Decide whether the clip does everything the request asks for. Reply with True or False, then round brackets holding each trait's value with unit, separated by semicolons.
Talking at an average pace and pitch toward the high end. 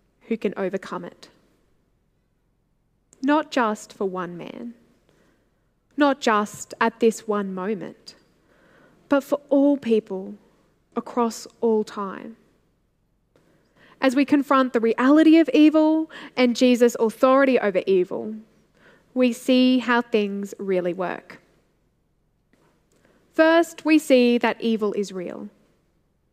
False (105 wpm; 235 Hz)